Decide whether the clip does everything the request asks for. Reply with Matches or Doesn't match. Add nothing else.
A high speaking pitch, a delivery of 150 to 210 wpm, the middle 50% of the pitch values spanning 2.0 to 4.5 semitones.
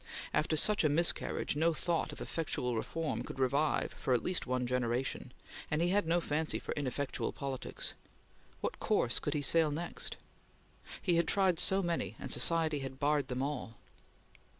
Doesn't match